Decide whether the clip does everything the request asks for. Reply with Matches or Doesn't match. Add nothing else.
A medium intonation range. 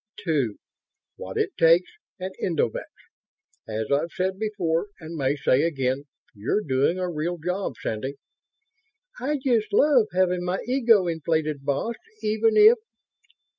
Doesn't match